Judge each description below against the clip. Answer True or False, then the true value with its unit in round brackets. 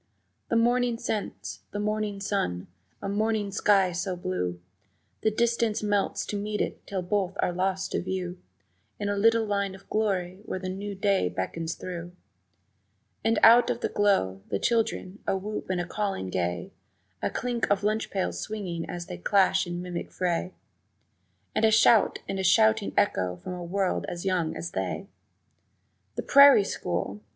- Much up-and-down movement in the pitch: False (3.2 semitones)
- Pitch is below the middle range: False (195 Hz)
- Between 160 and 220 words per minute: True (165 wpm)